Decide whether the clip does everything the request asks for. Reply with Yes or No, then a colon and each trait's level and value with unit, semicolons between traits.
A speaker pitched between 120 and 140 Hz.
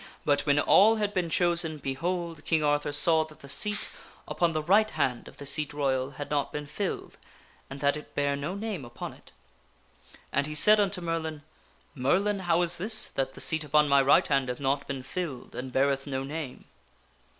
No: medium, 150 Hz